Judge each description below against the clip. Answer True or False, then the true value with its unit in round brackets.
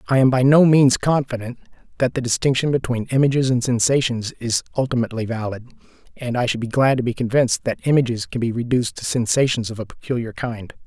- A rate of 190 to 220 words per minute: True (195 wpm)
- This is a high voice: False (125 Hz)